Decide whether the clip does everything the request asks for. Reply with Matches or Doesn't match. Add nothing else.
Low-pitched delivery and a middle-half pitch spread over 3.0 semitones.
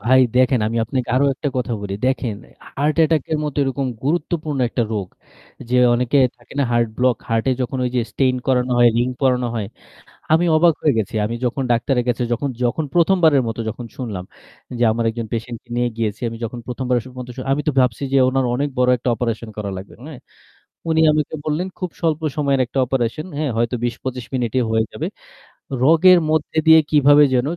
Matches